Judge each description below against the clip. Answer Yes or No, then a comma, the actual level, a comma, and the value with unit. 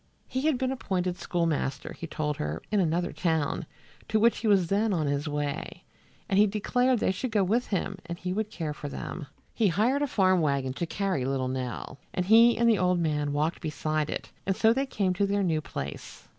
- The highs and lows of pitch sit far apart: Yes, wide, 5.8 semitones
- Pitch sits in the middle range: Yes, medium, 180 Hz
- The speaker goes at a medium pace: No, fast, 215 wpm